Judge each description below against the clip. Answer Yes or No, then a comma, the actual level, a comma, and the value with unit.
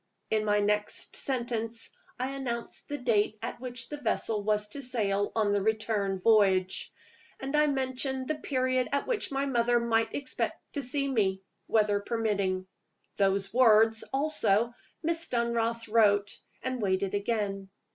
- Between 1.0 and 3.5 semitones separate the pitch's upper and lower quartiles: No, average, 3.9 semitones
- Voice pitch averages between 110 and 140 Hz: No, high, 225 Hz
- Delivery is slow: No, average, 145 wpm